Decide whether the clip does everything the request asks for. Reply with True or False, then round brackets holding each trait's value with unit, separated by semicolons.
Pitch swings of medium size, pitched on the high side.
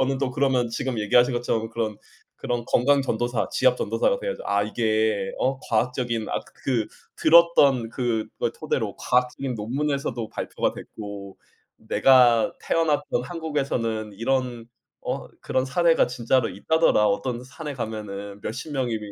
False (3.6 semitones; 125 Hz)